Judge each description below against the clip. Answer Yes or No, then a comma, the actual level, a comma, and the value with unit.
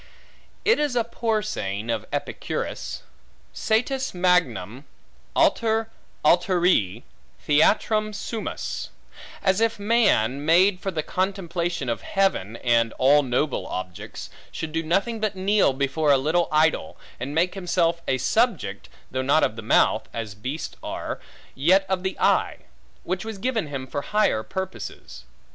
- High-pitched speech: No, medium, 170 Hz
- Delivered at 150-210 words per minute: No, average, 140 wpm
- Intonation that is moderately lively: No, wide, 7.2 semitones